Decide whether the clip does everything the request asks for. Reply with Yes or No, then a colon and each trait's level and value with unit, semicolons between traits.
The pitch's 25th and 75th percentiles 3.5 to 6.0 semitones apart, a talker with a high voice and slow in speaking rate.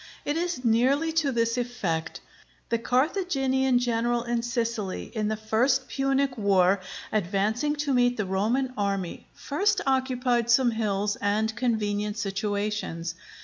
Yes: average, 3.9 semitones; high, 235 Hz; slow, 130 wpm